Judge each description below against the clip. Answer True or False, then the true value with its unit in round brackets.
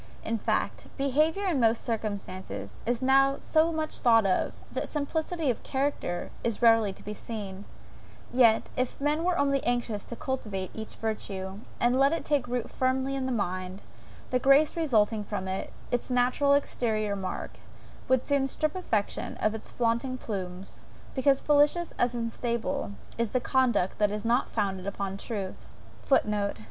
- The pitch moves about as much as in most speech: True (4.7 semitones)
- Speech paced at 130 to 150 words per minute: False (160 wpm)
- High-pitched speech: True (240 Hz)